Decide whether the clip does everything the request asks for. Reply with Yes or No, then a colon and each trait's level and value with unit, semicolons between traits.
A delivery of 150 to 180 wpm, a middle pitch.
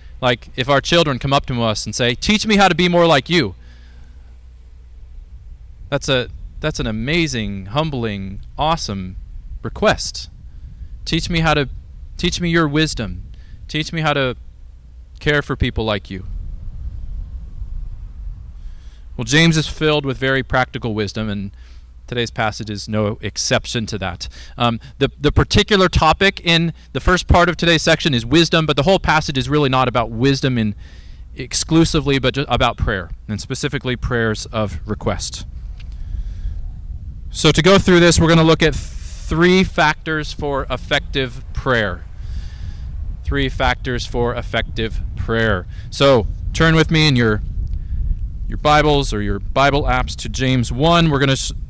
No: average, 155 wpm; low, 115 Hz